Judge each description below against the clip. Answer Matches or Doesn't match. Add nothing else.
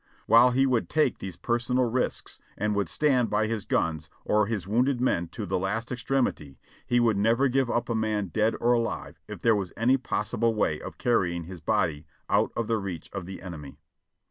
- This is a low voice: Matches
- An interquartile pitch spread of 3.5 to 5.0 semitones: Matches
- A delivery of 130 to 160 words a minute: Doesn't match